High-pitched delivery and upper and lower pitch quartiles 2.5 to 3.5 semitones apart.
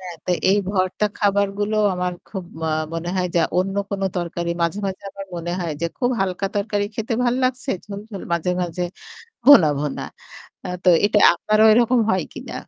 Yes: high, 195 Hz; average, 2.9 semitones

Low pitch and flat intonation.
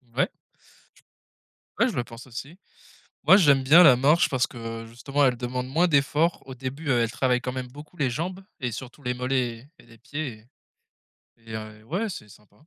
No: low, 130 Hz; average, 3.6 semitones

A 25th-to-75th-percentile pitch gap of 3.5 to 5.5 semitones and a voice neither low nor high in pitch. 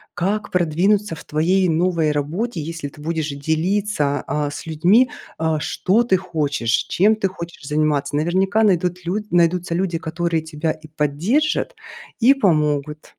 Yes: average, 3.9 semitones; medium, 170 Hz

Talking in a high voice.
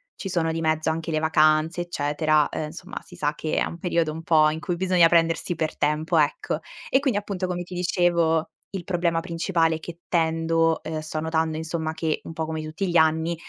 No: medium, 165 Hz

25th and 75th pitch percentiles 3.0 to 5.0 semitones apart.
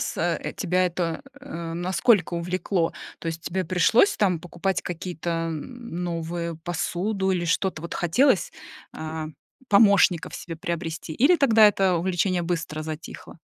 No: narrow, 2.5 semitones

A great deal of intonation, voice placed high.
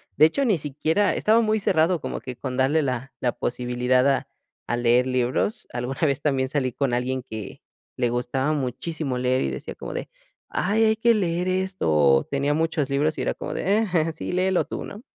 No: wide, 6.0 semitones; medium, 140 Hz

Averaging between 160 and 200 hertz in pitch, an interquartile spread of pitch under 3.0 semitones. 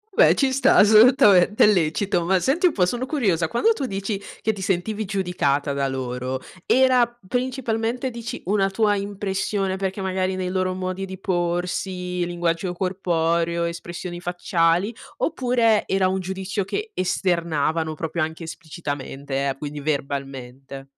No: medium, 185 Hz; average, 3.9 semitones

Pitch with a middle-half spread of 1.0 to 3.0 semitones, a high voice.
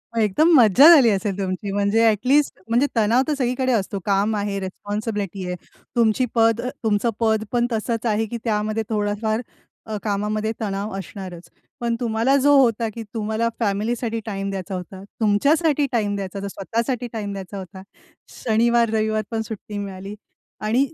Yes: narrow, 2.6 semitones; high, 215 Hz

